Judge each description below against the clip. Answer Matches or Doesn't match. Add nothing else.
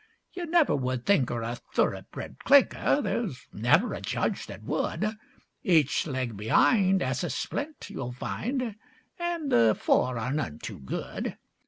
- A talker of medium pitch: Matches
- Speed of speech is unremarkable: Matches